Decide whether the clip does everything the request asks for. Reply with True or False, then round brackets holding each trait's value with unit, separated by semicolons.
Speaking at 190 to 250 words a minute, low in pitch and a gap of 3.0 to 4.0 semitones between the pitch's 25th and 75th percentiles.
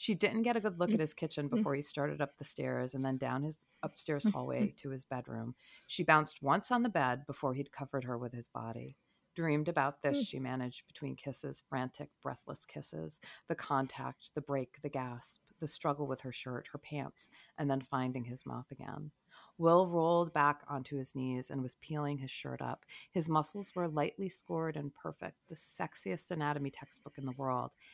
False (200 wpm; 145 Hz; 3.7 semitones)